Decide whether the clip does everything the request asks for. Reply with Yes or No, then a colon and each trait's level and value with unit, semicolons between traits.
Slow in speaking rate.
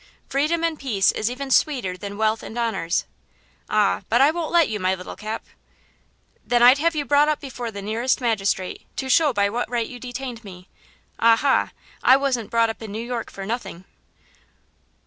No: average, 185 wpm